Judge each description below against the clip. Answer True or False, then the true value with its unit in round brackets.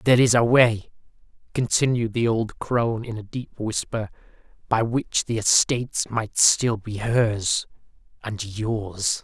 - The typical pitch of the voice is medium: False (115 Hz)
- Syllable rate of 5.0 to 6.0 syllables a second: False (4.0 syllables/s)